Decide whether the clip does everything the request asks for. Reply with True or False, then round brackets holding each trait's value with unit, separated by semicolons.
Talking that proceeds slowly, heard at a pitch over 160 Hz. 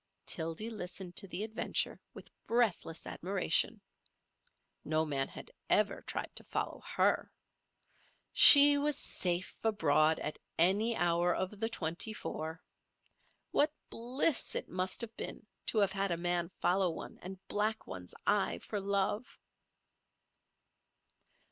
True (130 wpm; 190 Hz)